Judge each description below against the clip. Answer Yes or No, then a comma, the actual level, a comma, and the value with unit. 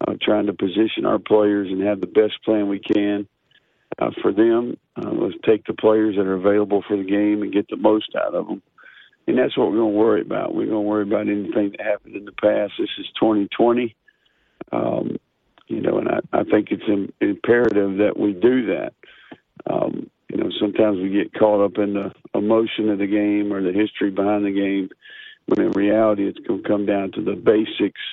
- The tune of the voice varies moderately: No, narrow, 1.8 semitones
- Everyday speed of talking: No, fast, 215 wpm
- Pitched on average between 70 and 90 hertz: No, low, 105 Hz